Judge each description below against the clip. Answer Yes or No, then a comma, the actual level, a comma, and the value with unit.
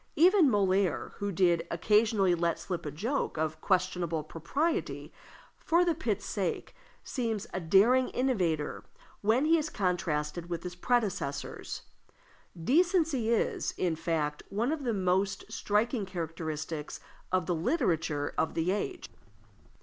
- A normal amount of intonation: No, wide, 6.0 semitones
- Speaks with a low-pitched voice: No, high, 190 Hz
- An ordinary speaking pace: No, slow, 130 wpm